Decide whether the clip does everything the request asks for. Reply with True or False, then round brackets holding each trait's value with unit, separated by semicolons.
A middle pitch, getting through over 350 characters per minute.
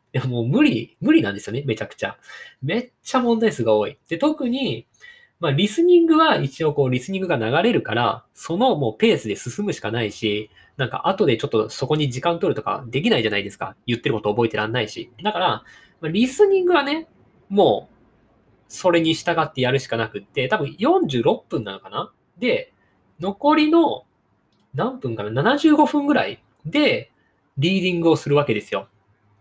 False (165 Hz; 345 characters per minute)